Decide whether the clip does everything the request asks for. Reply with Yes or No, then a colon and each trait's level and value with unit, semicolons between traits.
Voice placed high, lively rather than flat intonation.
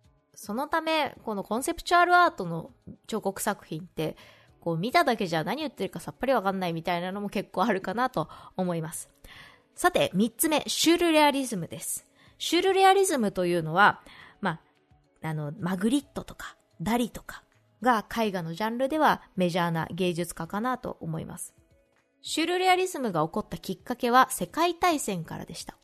Yes: high, 210 Hz; wide, 7.8 semitones